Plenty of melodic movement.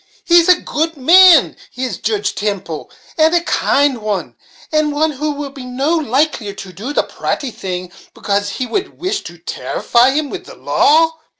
Yes: wide, 6.9 semitones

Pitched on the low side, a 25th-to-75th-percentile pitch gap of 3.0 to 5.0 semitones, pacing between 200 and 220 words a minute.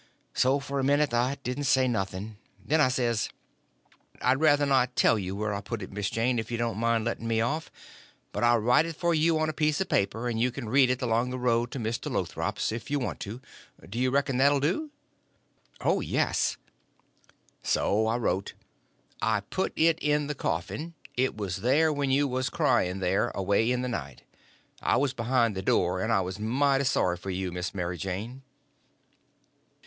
Yes: low, 120 Hz; average, 4.4 semitones; fast, 205 wpm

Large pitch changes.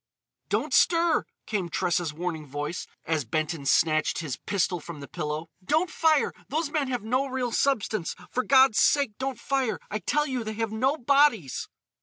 Yes: wide, 8.8 semitones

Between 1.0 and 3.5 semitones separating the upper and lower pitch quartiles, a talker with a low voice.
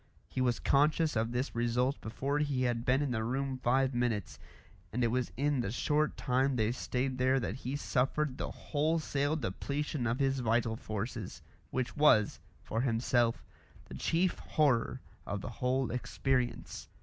Yes: average, 2.8 semitones; low, 130 Hz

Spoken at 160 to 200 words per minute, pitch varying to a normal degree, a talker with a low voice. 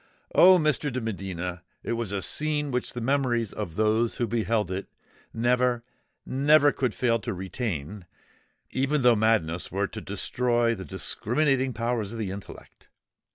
No: average, 145 wpm; average, 4.1 semitones; low, 115 Hz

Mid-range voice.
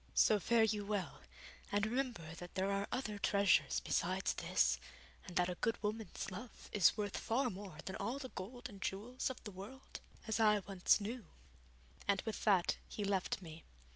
No: high, 205 Hz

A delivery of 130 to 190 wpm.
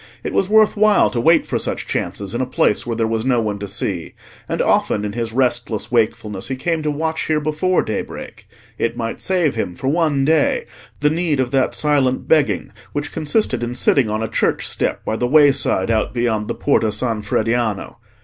No: fast, 205 wpm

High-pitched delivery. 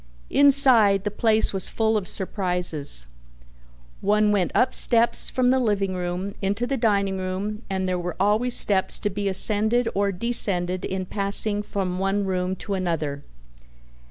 Yes: high, 200 Hz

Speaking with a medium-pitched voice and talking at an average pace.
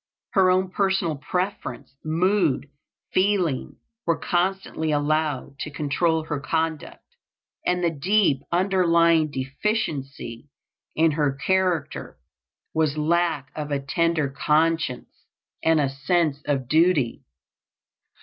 No: medium, 160 Hz; slow, 110 wpm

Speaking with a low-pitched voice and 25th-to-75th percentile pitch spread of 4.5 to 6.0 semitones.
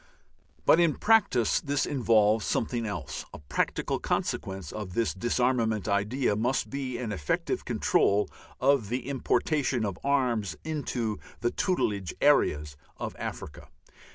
Yes: low, 115 Hz; average, 5.0 semitones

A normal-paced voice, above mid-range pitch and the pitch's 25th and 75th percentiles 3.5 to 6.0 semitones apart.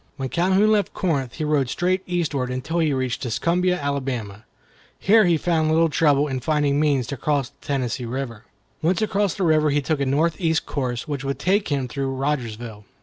No: average, 190 wpm; medium, 145 Hz; average, 4.3 semitones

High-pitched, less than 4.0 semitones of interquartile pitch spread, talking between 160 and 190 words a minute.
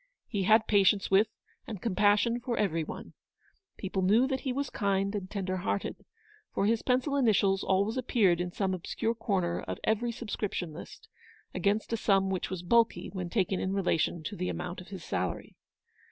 Yes: high, 200 Hz; average, 3.3 semitones; average, 180 wpm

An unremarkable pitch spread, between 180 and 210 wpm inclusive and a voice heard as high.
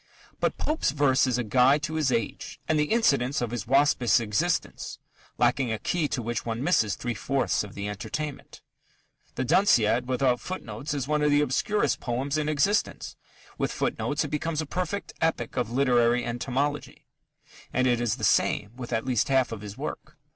No: average, 3.9 semitones; average, 185 wpm; low, 130 Hz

